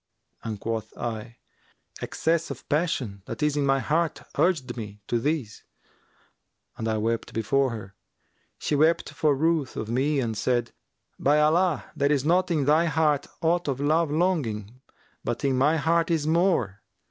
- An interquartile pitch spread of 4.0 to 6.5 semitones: Yes, wide, 5.5 semitones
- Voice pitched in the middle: Yes, medium, 145 Hz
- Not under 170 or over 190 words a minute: No, average, 160 wpm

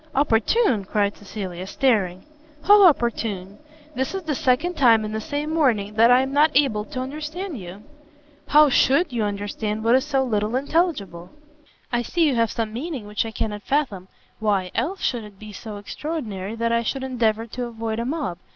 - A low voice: No, high, 230 Hz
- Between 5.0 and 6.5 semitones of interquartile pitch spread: Yes, average, 5.3 semitones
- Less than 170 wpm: No, average, 185 wpm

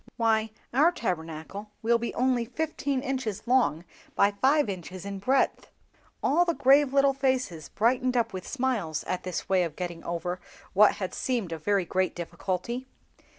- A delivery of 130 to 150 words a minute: No, average, 160 wpm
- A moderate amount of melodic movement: No, wide, 6.1 semitones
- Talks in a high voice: Yes, high, 220 Hz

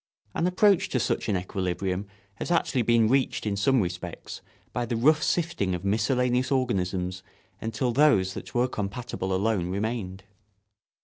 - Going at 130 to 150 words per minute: Yes, average, 145 wpm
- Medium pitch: No, low, 110 Hz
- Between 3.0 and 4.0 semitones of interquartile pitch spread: No, average, 5.3 semitones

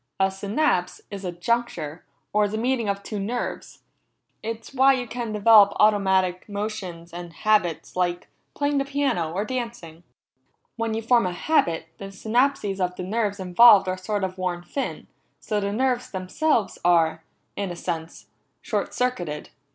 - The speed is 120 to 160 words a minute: Yes, average, 155 wpm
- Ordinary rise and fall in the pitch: Yes, average, 4.4 semitones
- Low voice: No, high, 200 Hz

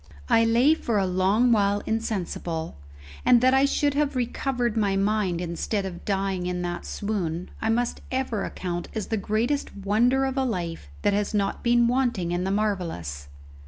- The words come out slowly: No, average, 175 wpm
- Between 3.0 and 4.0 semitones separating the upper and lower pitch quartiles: No, average, 4.8 semitones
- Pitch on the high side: Yes, high, 210 Hz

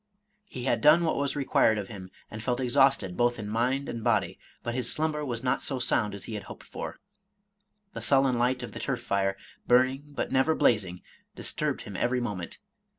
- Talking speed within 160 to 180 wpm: No, average, 200 wpm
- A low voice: Yes, low, 120 Hz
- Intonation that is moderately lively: Yes, average, 3.9 semitones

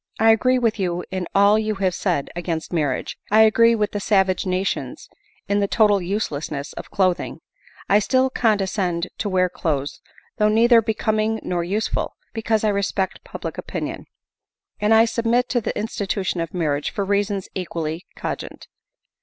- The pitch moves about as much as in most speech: Yes, average, 3.4 semitones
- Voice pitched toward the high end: Yes, high, 200 Hz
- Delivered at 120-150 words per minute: No, average, 160 wpm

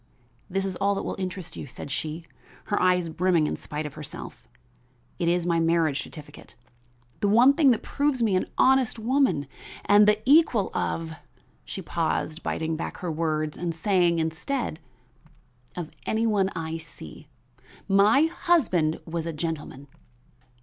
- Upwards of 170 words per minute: No, average, 155 wpm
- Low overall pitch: No, medium, 175 Hz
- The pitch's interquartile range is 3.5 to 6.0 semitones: Yes, average, 4.8 semitones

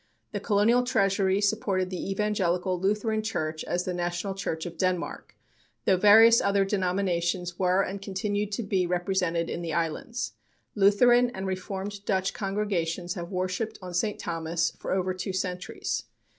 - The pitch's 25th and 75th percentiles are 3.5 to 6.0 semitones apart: No, narrow, 2.5 semitones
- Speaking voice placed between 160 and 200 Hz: Yes, high, 190 Hz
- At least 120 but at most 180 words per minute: Yes, average, 150 wpm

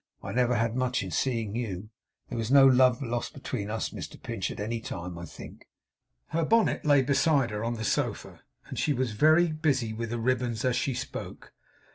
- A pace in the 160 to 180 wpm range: No, average, 200 wpm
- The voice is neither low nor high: No, low, 120 Hz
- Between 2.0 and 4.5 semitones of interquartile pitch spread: Yes, average, 3.4 semitones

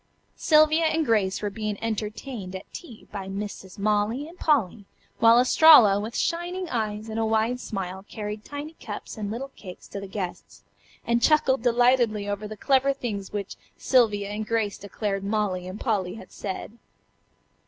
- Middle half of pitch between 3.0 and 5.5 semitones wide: Yes, average, 3.7 semitones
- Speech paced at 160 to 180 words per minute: Yes, average, 165 wpm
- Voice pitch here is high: Yes, high, 215 Hz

